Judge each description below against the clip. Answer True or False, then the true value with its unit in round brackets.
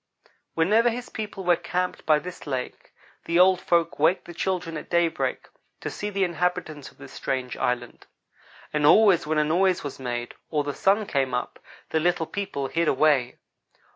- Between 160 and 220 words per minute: True (175 wpm)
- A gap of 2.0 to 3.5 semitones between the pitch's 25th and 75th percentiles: False (3.9 semitones)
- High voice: False (165 Hz)